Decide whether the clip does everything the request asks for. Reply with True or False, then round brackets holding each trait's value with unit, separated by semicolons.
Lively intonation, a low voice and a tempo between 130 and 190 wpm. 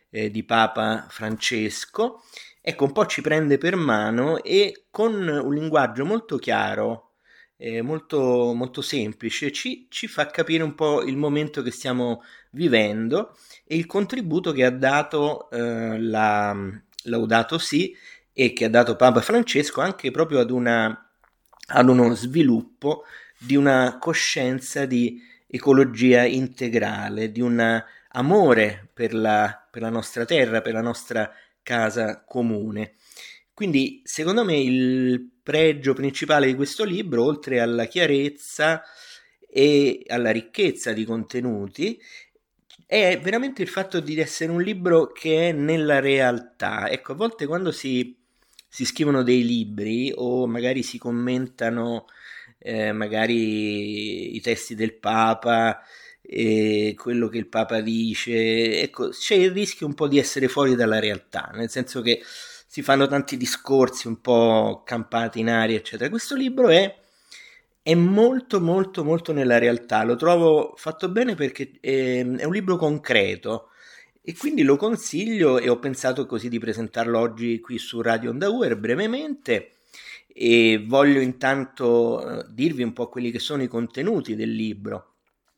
True (5.8 semitones; 130 Hz; 140 wpm)